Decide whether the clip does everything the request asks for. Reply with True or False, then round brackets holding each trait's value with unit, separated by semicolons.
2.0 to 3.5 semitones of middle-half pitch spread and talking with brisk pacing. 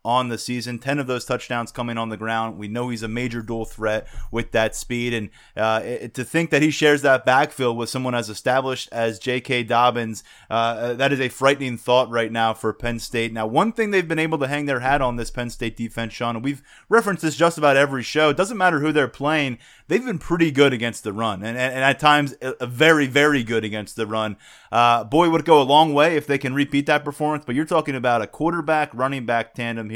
False (4.2 semitones; 240 wpm)